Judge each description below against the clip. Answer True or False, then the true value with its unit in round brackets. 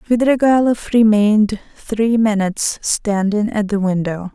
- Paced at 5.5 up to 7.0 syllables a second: False (4.2 syllables/s)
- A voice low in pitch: False (215 Hz)